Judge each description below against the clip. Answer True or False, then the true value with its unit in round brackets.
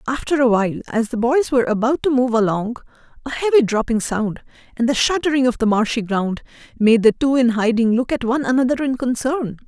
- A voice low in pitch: False (245 Hz)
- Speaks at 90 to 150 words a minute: False (205 wpm)